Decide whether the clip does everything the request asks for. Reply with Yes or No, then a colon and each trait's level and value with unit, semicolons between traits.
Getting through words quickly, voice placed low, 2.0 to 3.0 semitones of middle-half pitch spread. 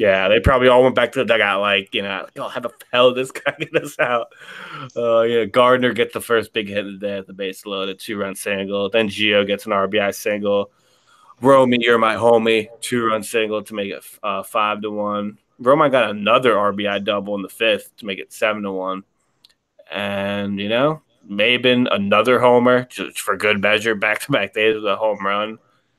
Yes: fast, 210 wpm; low, 105 Hz; average, 2.7 semitones